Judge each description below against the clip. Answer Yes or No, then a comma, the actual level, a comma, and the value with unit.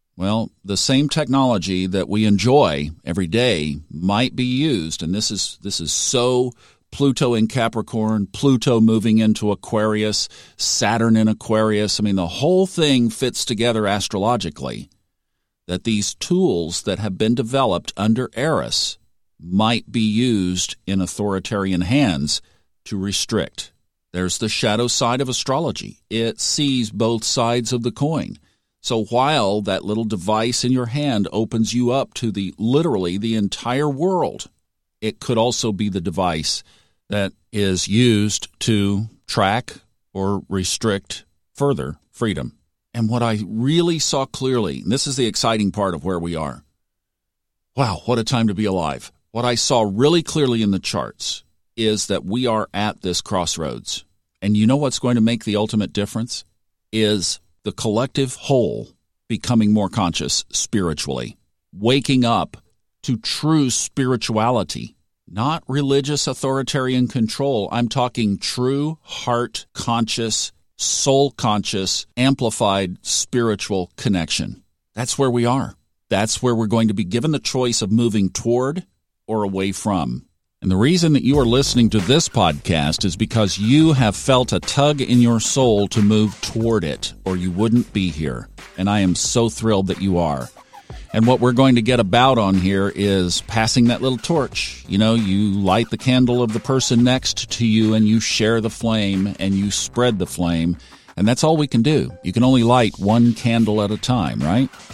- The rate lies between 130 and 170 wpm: Yes, average, 160 wpm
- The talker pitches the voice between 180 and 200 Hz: No, low, 110 Hz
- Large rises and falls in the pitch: No, average, 4.1 semitones